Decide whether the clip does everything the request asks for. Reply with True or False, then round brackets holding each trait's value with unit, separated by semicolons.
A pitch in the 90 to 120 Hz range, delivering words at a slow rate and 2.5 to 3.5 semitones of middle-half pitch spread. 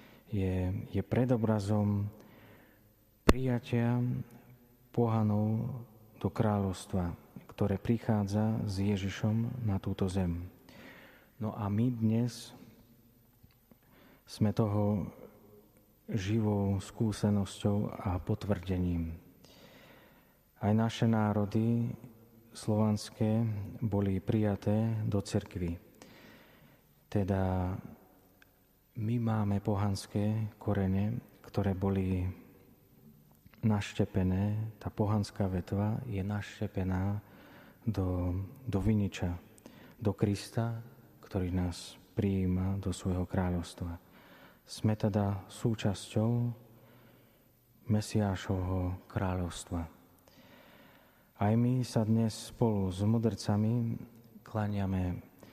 True (105 Hz; 75 wpm; 2.8 semitones)